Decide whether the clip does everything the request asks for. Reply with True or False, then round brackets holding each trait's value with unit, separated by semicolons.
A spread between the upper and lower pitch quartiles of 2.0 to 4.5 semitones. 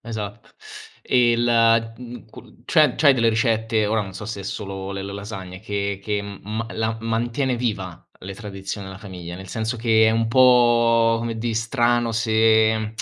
True (2.4 semitones)